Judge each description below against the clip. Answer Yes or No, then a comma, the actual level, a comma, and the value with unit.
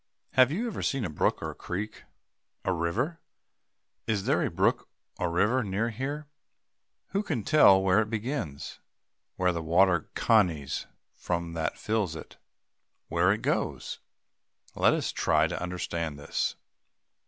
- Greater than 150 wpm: No, average, 140 wpm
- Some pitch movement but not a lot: No, wide, 6.2 semitones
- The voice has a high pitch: No, very low, 95 Hz